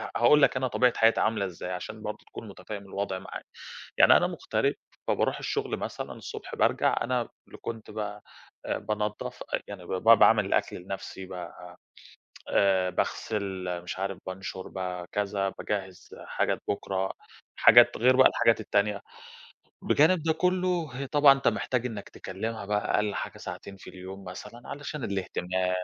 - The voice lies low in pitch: Yes, low, 105 Hz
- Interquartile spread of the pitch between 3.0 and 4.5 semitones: Yes, average, 3.9 semitones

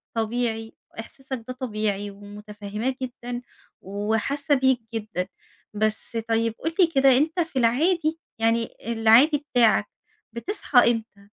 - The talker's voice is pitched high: Yes, high, 230 Hz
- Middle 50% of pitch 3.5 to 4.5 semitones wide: Yes, average, 3.8 semitones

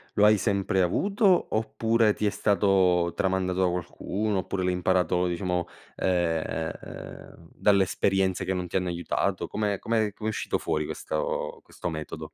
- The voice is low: Yes, very low, 95 Hz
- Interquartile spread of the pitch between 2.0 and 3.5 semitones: Yes, average, 2.7 semitones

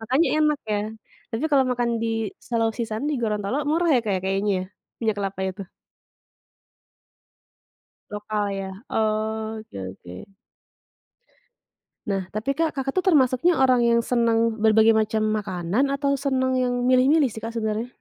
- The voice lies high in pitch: Yes, high, 230 Hz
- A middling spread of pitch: Yes, average, 3.4 semitones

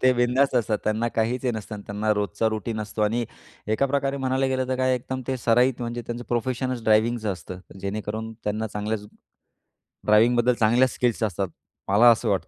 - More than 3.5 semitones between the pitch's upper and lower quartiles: No, average, 2.8 semitones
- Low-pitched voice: Yes, low, 115 Hz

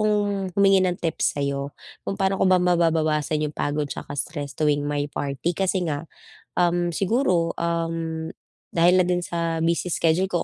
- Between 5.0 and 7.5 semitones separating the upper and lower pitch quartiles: No, average, 2.8 semitones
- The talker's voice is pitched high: No, medium, 165 Hz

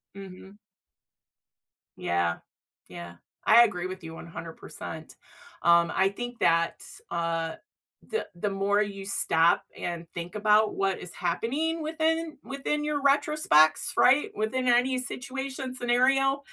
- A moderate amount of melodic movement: No, wide, 7.9 semitones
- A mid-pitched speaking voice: No, high, 210 Hz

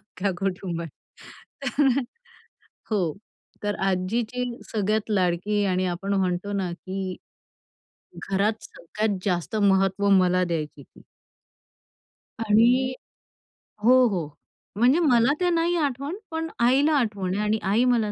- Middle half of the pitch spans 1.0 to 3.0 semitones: No, average, 4.7 semitones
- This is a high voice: Yes, high, 205 Hz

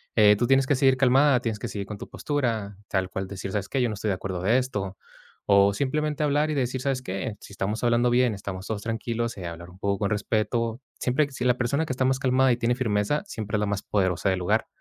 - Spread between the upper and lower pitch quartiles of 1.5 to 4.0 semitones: No, average, 4.6 semitones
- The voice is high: No, low, 115 Hz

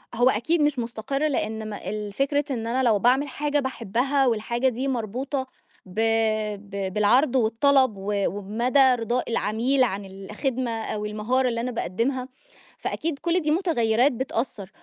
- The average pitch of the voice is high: Yes, high, 240 Hz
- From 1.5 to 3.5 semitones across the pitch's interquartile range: No, average, 3.9 semitones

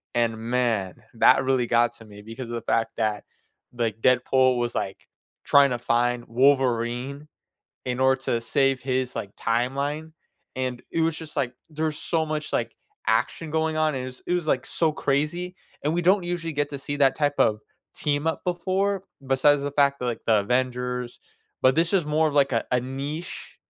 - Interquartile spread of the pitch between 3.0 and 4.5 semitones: Yes, average, 4.1 semitones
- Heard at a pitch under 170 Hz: Yes, low, 135 Hz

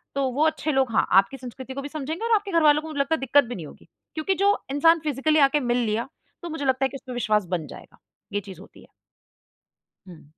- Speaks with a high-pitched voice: Yes, very high, 275 Hz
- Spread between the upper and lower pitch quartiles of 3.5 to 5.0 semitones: Yes, average, 4.3 semitones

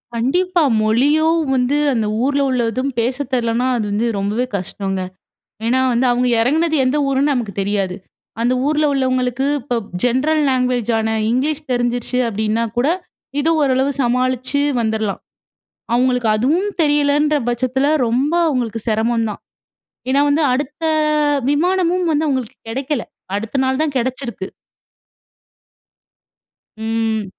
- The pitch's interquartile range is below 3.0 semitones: No, average, 3.9 semitones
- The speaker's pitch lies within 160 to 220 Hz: No, very high, 255 Hz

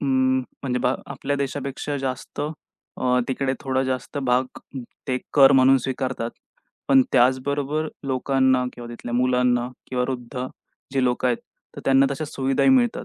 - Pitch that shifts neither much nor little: No, narrow, 1.4 semitones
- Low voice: Yes, low, 130 Hz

